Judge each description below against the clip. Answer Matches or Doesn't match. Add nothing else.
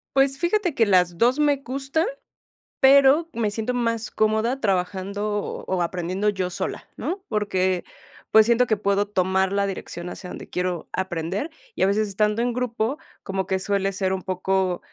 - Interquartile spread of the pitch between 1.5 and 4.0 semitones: Doesn't match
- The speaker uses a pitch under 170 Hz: Doesn't match